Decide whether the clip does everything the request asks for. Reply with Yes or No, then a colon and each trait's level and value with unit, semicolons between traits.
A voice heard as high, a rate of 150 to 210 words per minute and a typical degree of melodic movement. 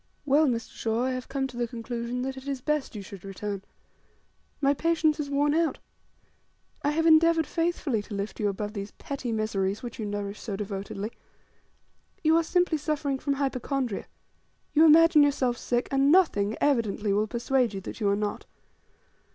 No: very high, 255 Hz; average, 175 wpm; wide, 5.8 semitones